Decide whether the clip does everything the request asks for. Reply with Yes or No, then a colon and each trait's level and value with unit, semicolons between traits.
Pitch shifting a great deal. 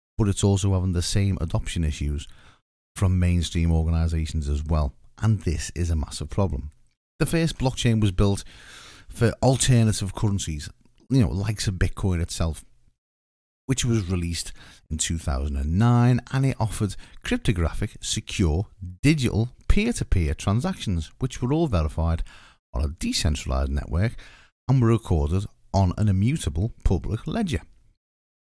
Yes: wide, 5.7 semitones